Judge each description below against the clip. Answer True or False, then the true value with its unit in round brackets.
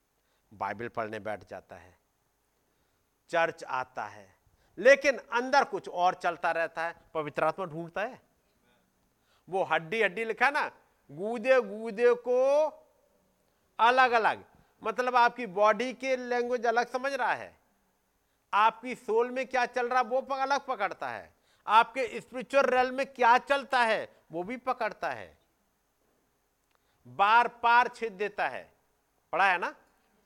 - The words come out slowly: False (135 wpm)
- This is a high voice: True (235 Hz)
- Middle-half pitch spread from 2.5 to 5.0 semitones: False (5.6 semitones)